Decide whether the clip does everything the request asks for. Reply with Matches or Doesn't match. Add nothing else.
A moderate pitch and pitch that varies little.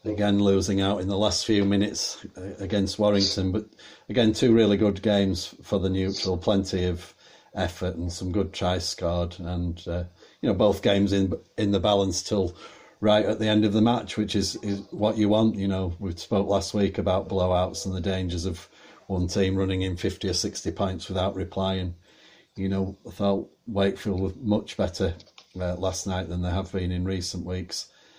Doesn't match